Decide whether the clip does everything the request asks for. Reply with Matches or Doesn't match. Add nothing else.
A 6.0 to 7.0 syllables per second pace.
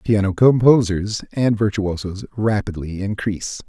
Doesn't match